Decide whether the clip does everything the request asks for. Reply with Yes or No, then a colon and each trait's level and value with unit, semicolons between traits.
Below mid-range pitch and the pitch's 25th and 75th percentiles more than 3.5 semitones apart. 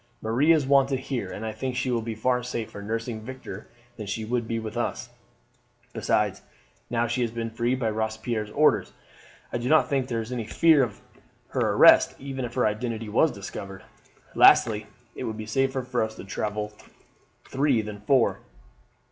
No: low, 115 Hz; average, 2.9 semitones